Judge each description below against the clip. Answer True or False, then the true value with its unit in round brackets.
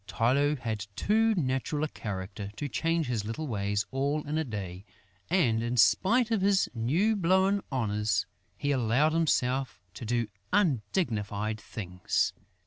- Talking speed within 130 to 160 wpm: True (140 wpm)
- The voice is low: True (130 Hz)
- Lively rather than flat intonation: True (7.3 semitones)